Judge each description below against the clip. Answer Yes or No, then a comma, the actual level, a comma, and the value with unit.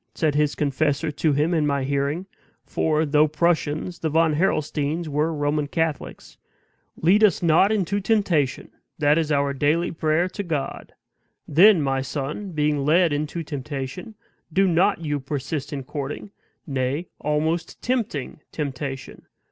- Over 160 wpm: No, average, 140 wpm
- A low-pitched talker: No, medium, 155 Hz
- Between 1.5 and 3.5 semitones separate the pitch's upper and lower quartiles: Yes, average, 2.9 semitones